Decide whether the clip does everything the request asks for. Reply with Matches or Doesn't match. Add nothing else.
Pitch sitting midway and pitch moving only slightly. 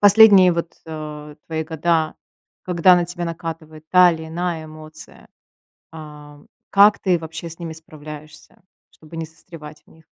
Matches